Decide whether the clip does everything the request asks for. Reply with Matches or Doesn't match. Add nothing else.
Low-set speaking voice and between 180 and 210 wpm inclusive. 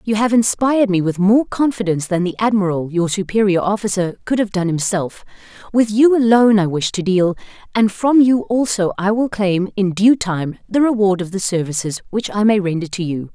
Doesn't match